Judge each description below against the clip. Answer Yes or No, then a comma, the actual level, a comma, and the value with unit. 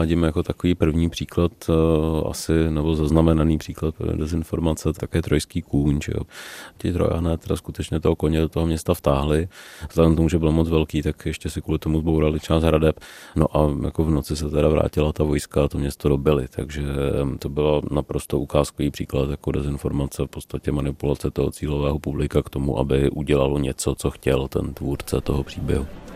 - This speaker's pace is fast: Yes, fast, 175 wpm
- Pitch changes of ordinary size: No, narrow, 2.1 semitones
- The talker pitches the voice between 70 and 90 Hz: Yes, very low, 75 Hz